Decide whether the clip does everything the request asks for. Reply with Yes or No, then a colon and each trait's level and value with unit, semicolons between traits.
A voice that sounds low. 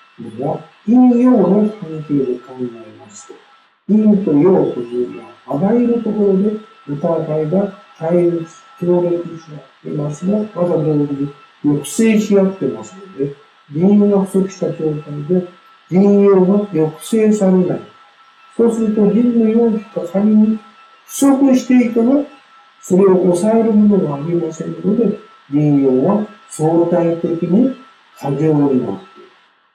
No: high, 190 Hz